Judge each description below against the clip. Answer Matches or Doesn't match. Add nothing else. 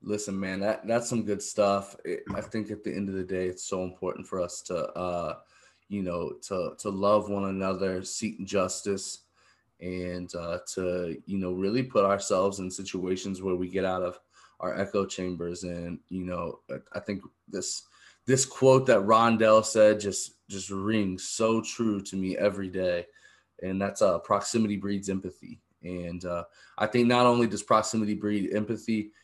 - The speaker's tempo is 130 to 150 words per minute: Doesn't match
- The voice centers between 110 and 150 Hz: Doesn't match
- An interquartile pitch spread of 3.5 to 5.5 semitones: Doesn't match